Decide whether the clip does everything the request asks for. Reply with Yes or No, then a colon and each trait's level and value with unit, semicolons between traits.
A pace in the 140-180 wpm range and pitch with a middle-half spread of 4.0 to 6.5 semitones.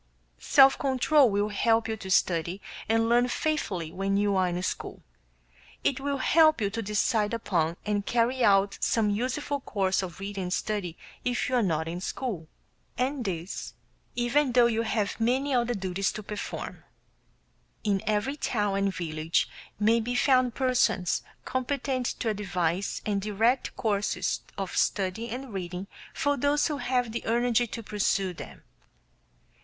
Yes: average, 155 wpm; average, 4.3 semitones